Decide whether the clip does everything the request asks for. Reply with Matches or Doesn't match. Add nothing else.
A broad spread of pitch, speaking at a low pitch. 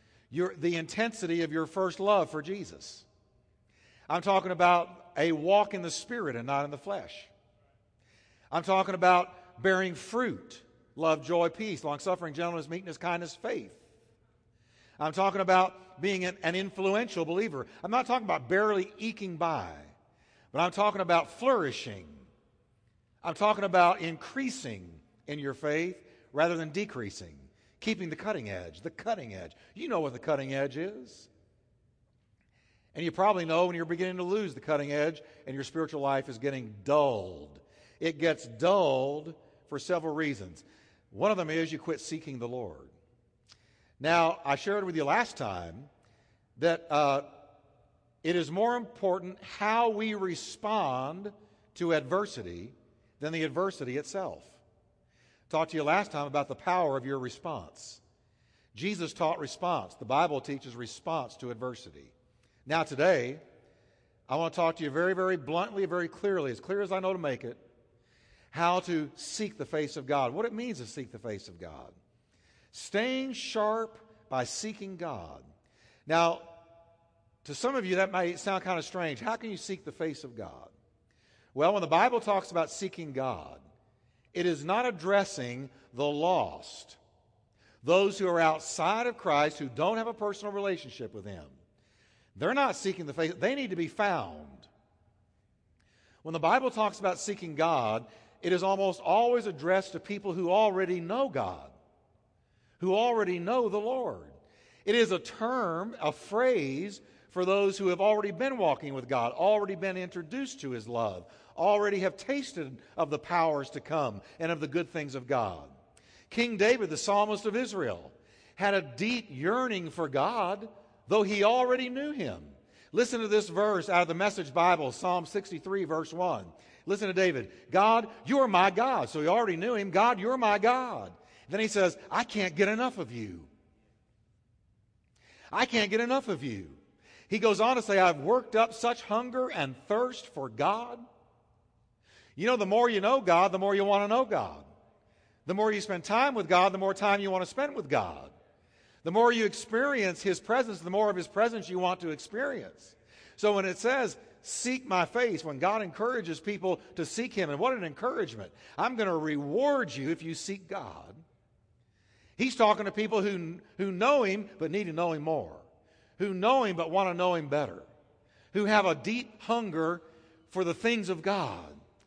Doesn't match